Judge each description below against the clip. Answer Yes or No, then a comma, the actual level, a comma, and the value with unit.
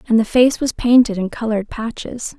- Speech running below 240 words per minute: Yes, average, 200 wpm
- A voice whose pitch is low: No, high, 230 Hz